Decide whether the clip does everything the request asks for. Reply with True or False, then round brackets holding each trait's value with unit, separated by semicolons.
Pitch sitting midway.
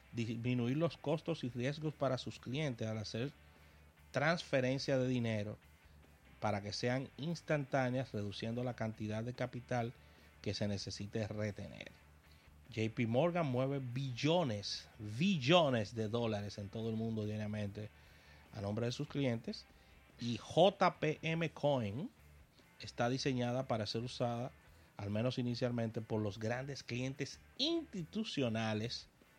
False (120 Hz)